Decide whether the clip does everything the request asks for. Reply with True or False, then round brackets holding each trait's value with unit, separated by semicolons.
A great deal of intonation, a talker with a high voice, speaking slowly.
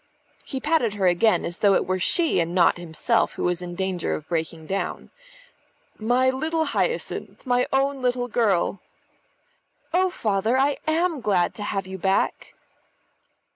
False (6.6 semitones; 215 Hz; 155 wpm)